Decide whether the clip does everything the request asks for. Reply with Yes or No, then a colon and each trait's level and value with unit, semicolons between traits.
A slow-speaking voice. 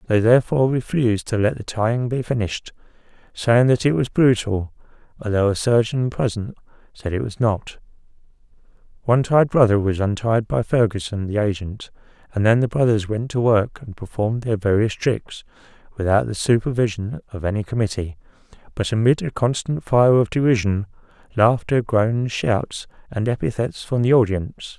No: average, 155 wpm